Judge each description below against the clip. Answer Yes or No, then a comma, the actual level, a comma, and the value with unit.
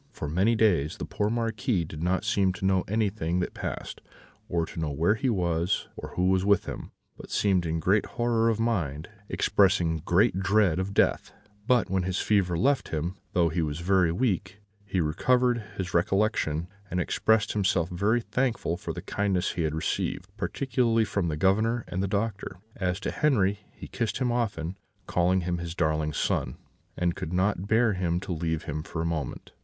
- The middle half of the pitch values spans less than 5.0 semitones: Yes, average, 4.2 semitones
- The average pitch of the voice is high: No, very low, 95 Hz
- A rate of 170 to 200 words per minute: Yes, average, 190 wpm